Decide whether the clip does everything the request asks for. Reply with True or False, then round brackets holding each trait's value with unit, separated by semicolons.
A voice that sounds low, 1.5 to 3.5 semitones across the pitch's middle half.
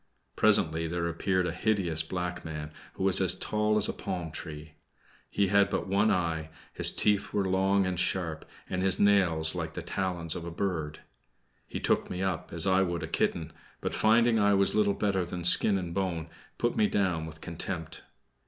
True (90 Hz; 3.1 semitones)